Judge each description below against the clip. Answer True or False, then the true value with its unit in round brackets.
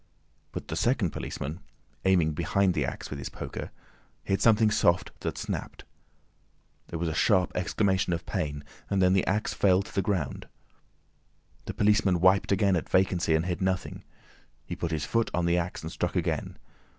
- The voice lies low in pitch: True (90 Hz)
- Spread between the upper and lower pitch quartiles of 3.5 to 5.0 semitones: False (2.8 semitones)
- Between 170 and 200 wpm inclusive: True (175 wpm)